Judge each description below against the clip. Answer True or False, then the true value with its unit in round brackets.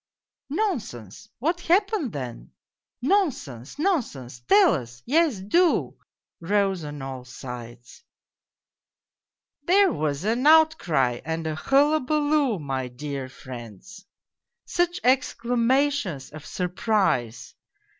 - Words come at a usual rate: False (105 wpm)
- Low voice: False (195 Hz)